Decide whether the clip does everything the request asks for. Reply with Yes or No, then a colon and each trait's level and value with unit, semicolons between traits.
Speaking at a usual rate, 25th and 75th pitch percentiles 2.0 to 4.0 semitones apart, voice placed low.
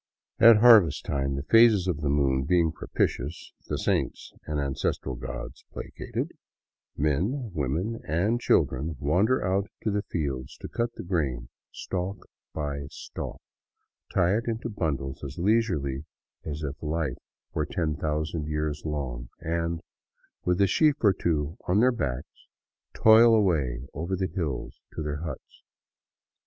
No: average, 145 wpm; wide, 5.6 semitones; very low, 80 Hz